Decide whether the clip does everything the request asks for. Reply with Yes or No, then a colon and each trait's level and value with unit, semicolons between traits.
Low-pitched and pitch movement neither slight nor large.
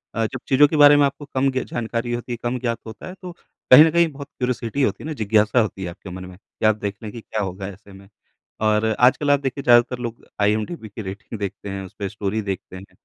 Yes: low, 115 Hz; average, 4.5 semitones